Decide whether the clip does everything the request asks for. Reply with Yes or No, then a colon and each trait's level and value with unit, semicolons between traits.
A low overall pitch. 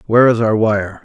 Yes: low, 110 Hz